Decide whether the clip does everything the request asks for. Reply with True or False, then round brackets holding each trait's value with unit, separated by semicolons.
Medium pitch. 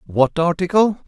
True (170 Hz)